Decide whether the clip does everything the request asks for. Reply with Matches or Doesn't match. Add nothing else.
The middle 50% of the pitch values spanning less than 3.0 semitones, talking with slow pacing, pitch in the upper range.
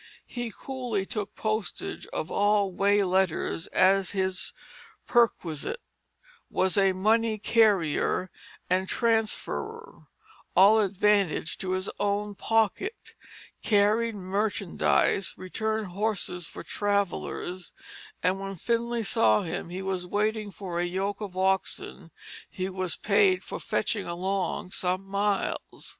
Matches